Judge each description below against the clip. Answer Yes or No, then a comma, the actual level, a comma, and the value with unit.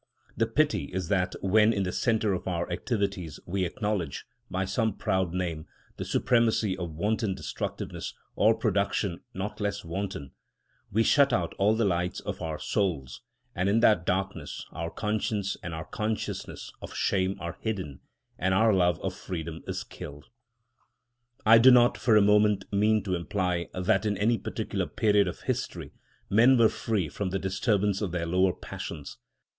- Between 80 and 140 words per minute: No, average, 165 wpm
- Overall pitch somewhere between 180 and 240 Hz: No, very low, 95 Hz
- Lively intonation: No, average, 3.3 semitones